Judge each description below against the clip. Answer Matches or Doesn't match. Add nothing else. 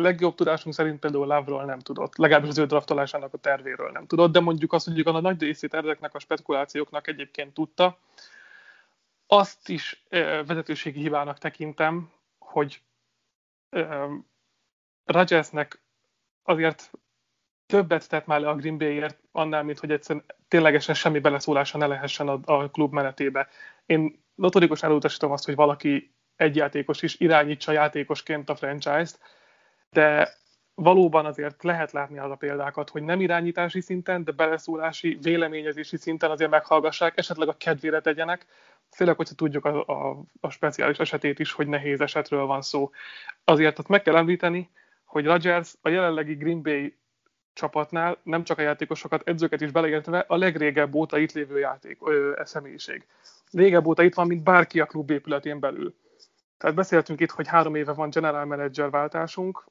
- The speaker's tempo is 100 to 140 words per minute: Doesn't match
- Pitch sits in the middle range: Matches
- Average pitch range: Doesn't match